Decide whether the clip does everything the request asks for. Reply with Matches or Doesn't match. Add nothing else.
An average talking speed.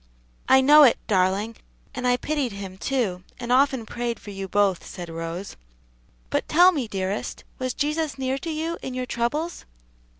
Matches